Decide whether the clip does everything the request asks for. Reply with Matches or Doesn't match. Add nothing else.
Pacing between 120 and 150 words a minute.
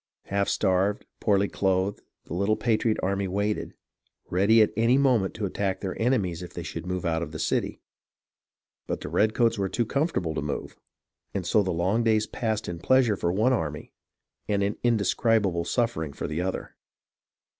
Doesn't match